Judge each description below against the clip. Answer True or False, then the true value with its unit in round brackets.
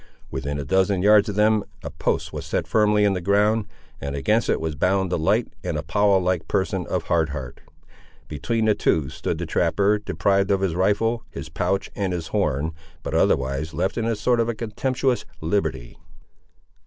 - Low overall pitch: True (95 Hz)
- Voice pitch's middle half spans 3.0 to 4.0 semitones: False (4.8 semitones)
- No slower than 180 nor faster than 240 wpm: True (185 wpm)